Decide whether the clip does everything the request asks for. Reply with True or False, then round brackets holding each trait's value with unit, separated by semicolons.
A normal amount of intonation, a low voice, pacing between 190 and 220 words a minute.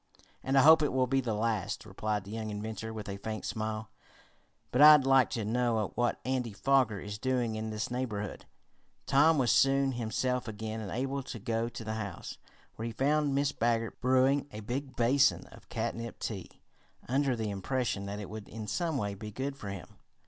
True (3.6 semitones; 115 Hz; 195 wpm)